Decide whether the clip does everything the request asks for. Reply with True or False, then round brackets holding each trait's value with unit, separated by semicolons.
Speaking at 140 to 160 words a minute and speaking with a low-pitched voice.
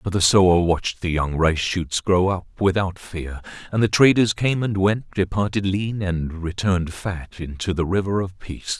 False (190 wpm; 95 Hz)